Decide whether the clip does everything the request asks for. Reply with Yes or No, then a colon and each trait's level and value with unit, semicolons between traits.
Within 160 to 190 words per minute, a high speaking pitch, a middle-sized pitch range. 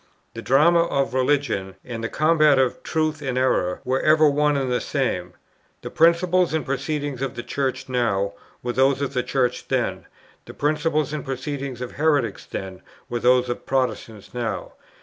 No: average, 170 wpm; low, 135 Hz; average, 3.4 semitones